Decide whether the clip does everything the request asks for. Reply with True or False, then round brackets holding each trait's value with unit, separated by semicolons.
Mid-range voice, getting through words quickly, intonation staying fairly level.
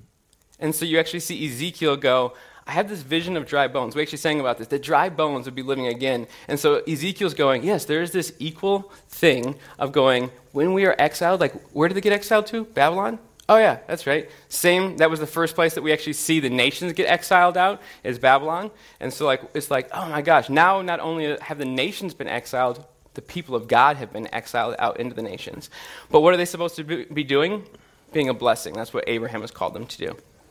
False (160 Hz; 230 wpm; 4.2 semitones)